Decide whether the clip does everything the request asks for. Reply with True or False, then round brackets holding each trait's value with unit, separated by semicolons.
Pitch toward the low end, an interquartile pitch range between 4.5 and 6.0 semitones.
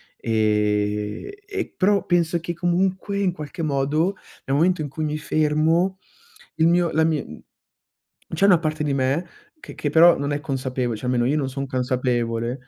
False (150 Hz; 5.1 semitones)